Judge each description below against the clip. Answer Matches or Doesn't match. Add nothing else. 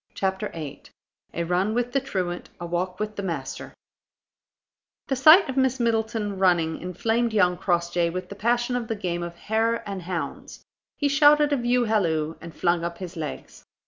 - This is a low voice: Doesn't match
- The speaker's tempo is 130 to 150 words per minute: Doesn't match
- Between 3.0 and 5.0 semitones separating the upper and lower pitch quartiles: Doesn't match